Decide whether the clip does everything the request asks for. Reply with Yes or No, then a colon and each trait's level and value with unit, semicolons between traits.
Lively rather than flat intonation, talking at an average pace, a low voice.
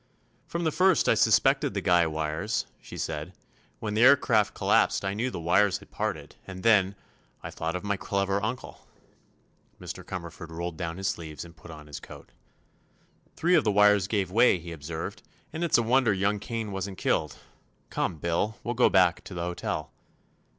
No: average, 4.3 semitones; average, 180 wpm; very low, 95 Hz